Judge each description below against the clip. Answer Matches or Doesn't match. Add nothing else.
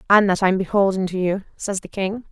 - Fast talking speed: Matches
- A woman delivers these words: Matches